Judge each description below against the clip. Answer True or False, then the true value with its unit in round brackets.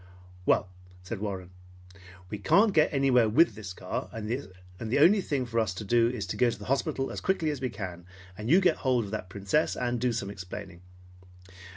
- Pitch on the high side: False (115 Hz)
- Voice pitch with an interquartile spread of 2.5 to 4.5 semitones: False (5.3 semitones)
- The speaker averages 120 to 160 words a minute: False (205 wpm)